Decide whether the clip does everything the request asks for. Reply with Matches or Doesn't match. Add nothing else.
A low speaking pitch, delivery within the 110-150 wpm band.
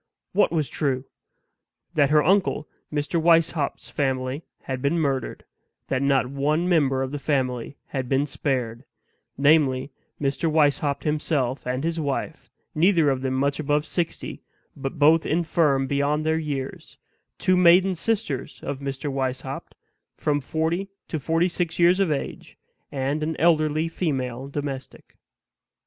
Doesn't match